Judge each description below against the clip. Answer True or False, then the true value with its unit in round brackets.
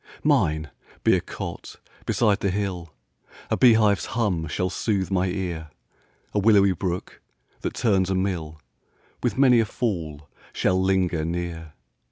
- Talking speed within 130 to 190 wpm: True (145 wpm)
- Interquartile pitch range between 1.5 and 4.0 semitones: True (3.3 semitones)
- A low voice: True (95 Hz)